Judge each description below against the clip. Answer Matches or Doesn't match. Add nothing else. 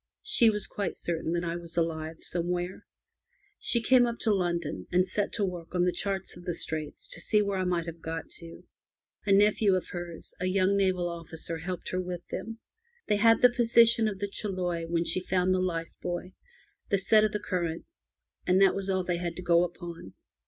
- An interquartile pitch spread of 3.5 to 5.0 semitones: Doesn't match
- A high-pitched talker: Doesn't match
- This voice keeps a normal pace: Doesn't match